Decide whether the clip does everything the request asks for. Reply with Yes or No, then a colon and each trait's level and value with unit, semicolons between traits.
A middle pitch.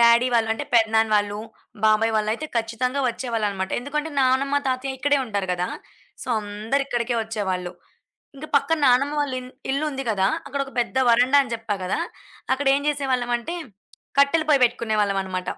No: high, 240 Hz